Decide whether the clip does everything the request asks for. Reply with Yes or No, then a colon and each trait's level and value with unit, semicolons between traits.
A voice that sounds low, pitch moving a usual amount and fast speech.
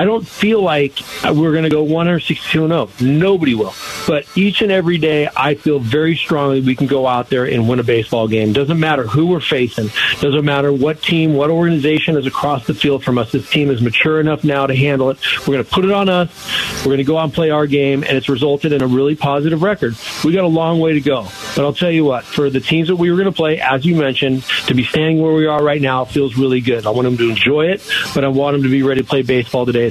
No: medium, 145 Hz; average, 3.3 semitones; fast, 270 wpm